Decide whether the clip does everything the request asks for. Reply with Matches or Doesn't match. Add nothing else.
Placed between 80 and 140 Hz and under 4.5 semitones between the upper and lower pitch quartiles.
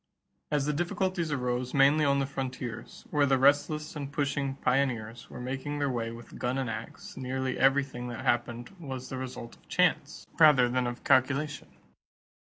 Matches